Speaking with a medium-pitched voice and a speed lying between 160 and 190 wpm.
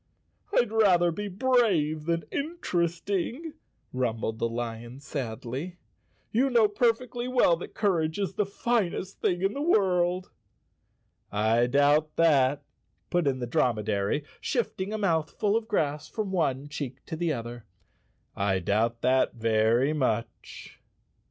No: medium, 160 Hz; slow, 135 wpm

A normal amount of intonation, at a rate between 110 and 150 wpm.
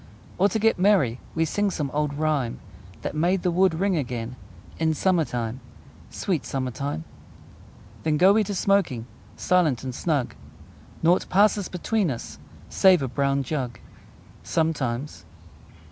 No: wide, 5.9 semitones; average, 140 wpm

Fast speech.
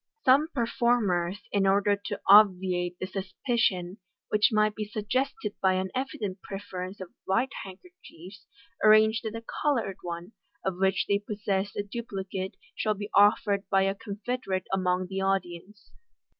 No: average, 145 wpm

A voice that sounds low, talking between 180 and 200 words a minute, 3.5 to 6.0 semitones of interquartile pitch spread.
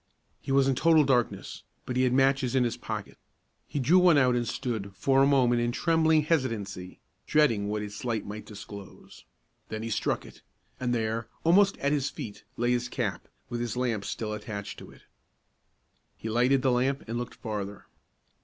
Yes: low, 120 Hz; average, 185 wpm; average, 3.8 semitones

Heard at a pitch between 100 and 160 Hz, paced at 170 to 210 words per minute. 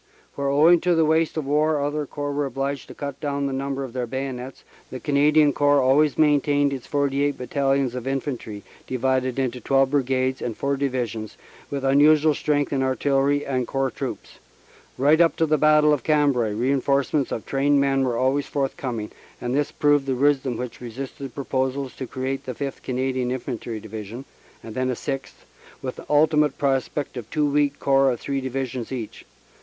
Yes: low, 135 Hz; average, 185 wpm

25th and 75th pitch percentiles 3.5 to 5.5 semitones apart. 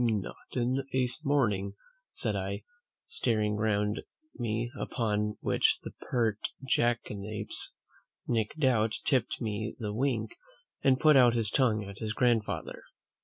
No: average, 2.9 semitones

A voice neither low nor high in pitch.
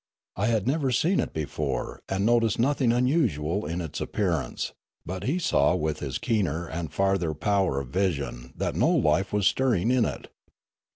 No: very low, 95 Hz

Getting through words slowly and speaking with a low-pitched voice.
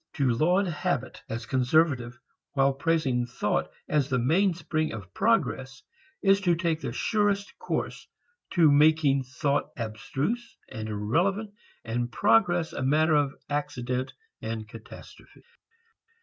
No: slow, 125 wpm; medium, 145 Hz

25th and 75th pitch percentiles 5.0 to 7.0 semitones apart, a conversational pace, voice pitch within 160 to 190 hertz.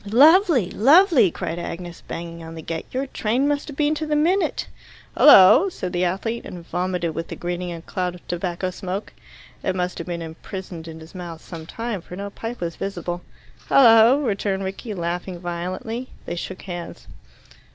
Yes: wide, 5.4 semitones; average, 180 wpm; medium, 185 Hz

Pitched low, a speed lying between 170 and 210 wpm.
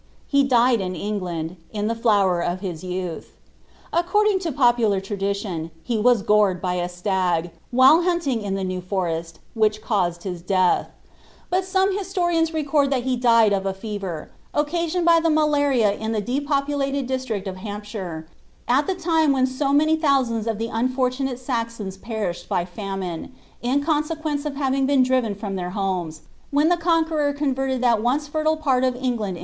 No: high, 240 Hz; average, 175 wpm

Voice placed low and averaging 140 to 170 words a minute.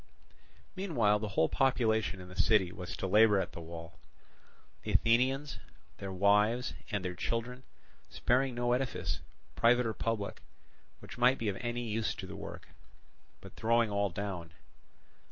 Yes: low, 110 Hz; average, 155 wpm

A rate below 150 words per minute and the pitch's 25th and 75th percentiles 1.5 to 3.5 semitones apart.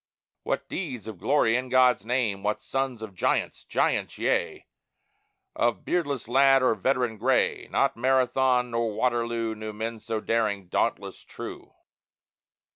Yes: slow, 135 wpm; average, 2.8 semitones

